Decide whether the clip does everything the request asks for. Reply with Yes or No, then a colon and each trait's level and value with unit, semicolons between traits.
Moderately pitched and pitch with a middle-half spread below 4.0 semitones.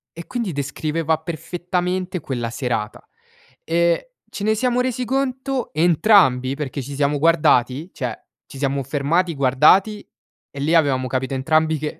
No: medium, 155 Hz; average, 4.8 semitones